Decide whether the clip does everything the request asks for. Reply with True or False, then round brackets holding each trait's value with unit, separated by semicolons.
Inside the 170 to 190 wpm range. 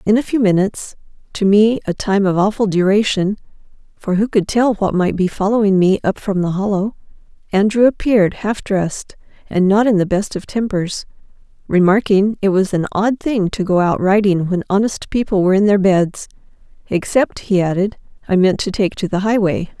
True (180 wpm)